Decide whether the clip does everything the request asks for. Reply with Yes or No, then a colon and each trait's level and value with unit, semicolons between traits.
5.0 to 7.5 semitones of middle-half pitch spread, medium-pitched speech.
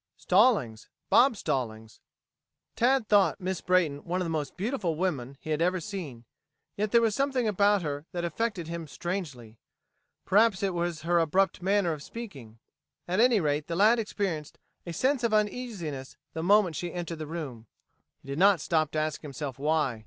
Yes: wide, 5.4 semitones; medium, 175 Hz